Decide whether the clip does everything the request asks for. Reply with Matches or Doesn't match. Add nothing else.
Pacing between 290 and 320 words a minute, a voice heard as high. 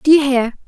Doesn't match